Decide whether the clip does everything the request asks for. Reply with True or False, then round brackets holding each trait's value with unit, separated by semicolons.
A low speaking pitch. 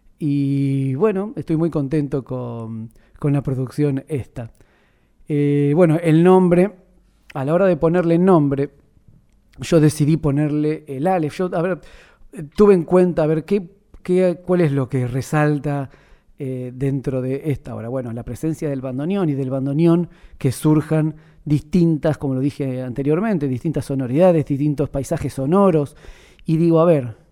False (150 Hz)